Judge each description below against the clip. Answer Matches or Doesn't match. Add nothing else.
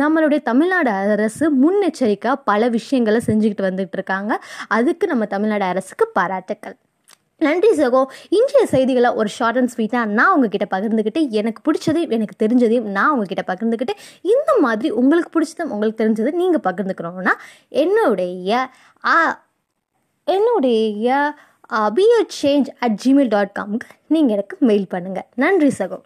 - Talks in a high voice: Matches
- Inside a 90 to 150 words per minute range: Matches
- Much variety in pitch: Matches